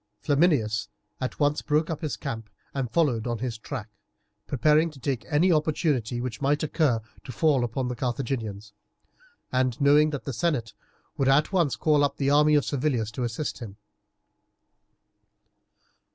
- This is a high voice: No, low, 135 Hz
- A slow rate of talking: No, average, 155 wpm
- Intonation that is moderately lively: Yes, average, 4.2 semitones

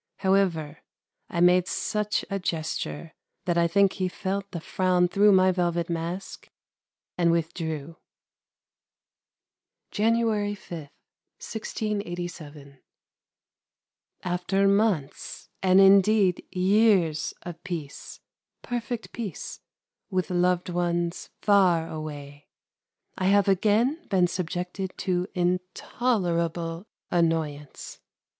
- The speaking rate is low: Yes, slow, 95 wpm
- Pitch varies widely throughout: No, average, 2.9 semitones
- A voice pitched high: No, medium, 180 Hz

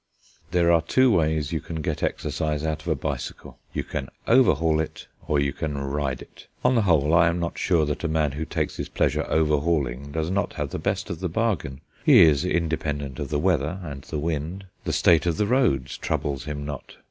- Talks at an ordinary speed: No, fast, 215 wpm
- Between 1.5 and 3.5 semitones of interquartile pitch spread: Yes, average, 2.8 semitones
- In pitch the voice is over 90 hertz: No, very low, 80 Hz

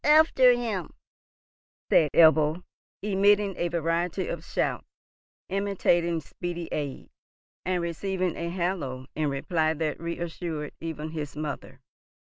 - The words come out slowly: Yes, slow, 115 wpm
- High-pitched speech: No, medium, 170 Hz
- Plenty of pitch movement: No, average, 3.0 semitones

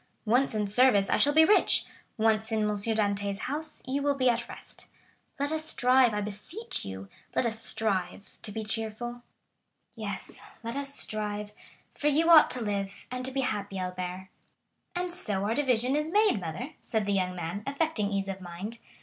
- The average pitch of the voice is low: No, high, 220 Hz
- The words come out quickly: No, average, 175 wpm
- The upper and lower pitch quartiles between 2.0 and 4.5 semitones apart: No, average, 5.3 semitones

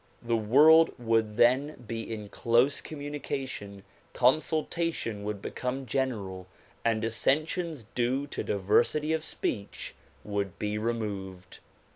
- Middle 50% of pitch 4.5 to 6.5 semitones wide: Yes, average, 5.3 semitones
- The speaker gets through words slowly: Yes, slow, 110 wpm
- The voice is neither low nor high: No, low, 115 Hz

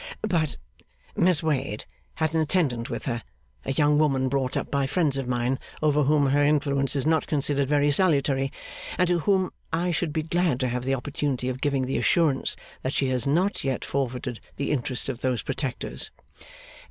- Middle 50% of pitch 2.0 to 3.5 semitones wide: Yes, average, 2.9 semitones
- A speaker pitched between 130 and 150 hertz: Yes, medium, 140 Hz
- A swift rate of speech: No, average, 190 wpm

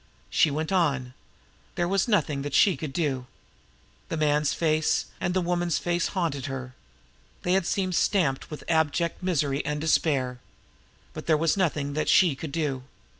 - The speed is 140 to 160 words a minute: No, average, 170 wpm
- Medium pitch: Yes, medium, 155 Hz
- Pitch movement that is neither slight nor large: Yes, average, 3.7 semitones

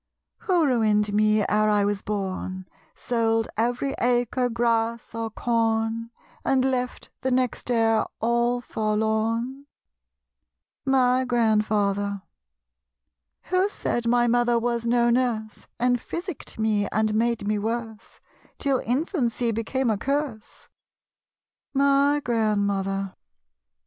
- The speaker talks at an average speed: No, slow, 110 wpm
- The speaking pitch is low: No, high, 230 Hz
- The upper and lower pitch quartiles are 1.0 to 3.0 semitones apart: Yes, narrow, 2.6 semitones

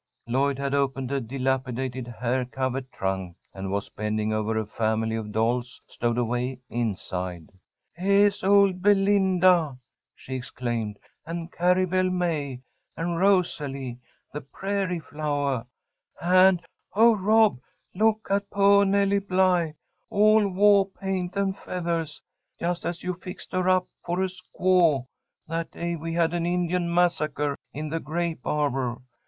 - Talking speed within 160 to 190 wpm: No, slow, 135 wpm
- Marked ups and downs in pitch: Yes, wide, 6.5 semitones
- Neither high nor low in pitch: Yes, medium, 165 Hz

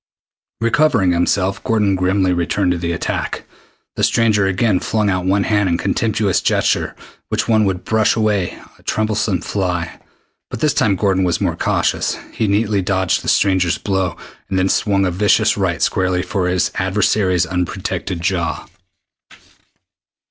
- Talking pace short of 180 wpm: Yes, average, 155 wpm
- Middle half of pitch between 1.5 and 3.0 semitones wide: Yes, narrow, 2.5 semitones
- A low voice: Yes, very low, 95 Hz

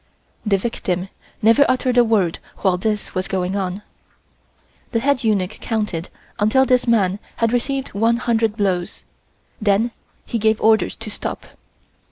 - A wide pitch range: No, average, 3.3 semitones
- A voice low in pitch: No, high, 220 Hz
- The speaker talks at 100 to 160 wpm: Yes, average, 145 wpm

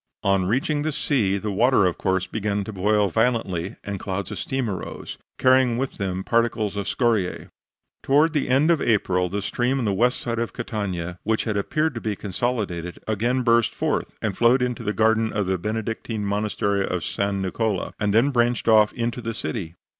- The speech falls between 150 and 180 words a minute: No, average, 190 wpm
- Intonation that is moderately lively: Yes, average, 3.4 semitones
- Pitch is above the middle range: No, low, 110 Hz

